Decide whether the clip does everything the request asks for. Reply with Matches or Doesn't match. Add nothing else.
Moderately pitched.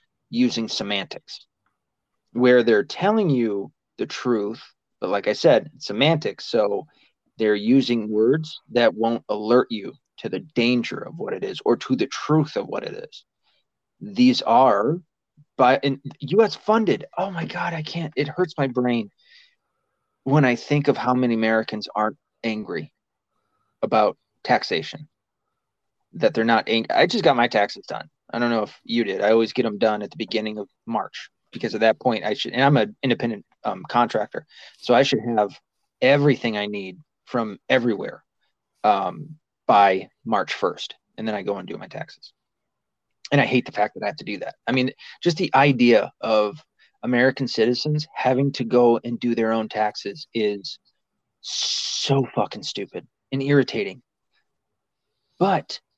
Doesn't match